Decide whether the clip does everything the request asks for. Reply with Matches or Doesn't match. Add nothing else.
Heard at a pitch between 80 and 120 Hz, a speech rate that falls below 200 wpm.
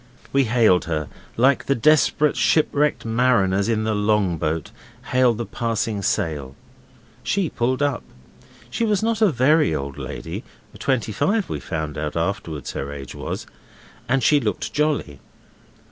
Matches